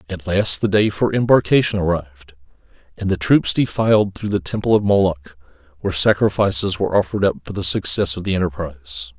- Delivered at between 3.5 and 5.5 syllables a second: No, 6.0 syllables/s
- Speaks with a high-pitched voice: No, very low, 95 Hz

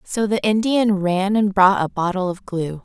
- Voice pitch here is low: No, high, 195 Hz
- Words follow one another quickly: Yes, fast, 210 wpm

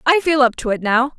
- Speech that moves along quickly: Yes, fast, 305 wpm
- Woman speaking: Yes, female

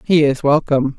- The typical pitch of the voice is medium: Yes, medium, 145 Hz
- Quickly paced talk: No, average, 185 wpm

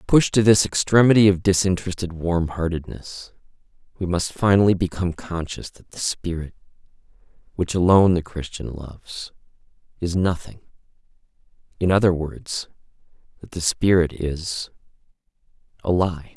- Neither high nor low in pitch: No, very low, 90 Hz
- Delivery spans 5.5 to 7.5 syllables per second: No, 4.9 syllables/s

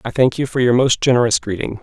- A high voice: No, low, 120 Hz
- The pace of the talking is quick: Yes, fast, 260 wpm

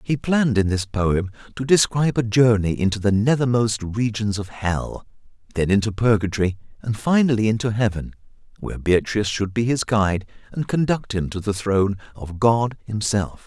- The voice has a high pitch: No, low, 110 Hz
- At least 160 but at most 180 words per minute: Yes, average, 165 wpm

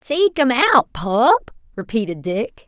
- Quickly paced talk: No, slow, 135 wpm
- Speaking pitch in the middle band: No, high, 245 Hz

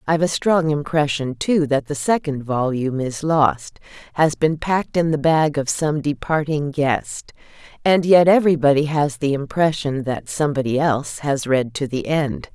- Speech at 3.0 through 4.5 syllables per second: No, 4.7 syllables/s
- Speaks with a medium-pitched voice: Yes, medium, 145 Hz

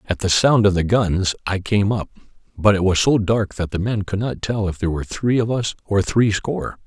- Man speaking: Yes, male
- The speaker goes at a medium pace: No, fast, 255 wpm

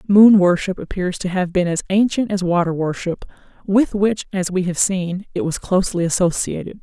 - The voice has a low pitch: No, medium, 185 Hz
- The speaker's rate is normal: Yes, average, 185 wpm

